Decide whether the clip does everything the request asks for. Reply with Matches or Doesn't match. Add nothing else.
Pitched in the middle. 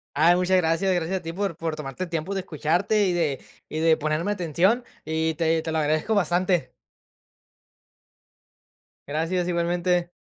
Matches